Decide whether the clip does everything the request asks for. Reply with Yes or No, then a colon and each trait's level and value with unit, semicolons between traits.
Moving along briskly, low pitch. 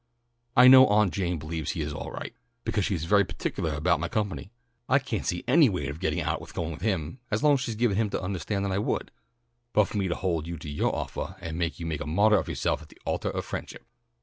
Yes: fast, 260 wpm; very low, 95 Hz